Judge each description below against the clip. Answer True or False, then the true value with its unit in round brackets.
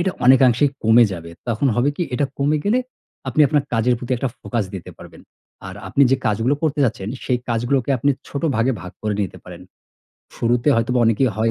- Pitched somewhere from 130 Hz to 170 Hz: False (120 Hz)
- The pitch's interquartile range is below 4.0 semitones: True (3.5 semitones)